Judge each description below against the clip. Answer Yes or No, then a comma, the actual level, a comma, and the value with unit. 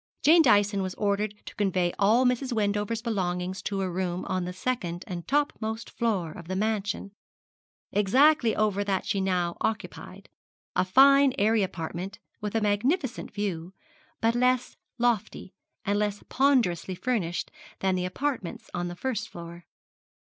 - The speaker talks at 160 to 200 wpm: No, average, 150 wpm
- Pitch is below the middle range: No, high, 205 Hz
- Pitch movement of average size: Yes, average, 4.0 semitones